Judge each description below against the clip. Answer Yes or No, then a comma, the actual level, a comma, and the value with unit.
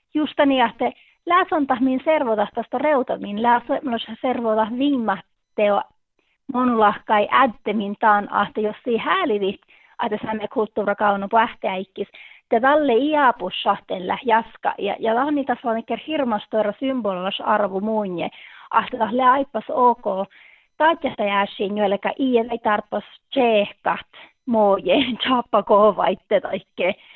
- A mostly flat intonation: No, average, 3.8 semitones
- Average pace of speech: Yes, average, 110 wpm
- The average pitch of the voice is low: No, high, 225 Hz